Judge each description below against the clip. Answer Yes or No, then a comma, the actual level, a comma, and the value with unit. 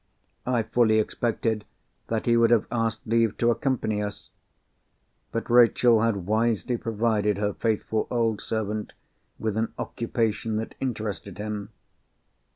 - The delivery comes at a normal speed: No, slow, 130 wpm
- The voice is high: No, low, 110 Hz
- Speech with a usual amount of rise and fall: No, narrow, 1.5 semitones